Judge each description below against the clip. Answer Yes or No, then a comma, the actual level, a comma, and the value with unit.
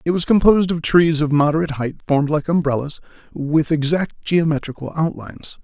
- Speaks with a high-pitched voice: No, medium, 155 Hz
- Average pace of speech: Yes, average, 160 wpm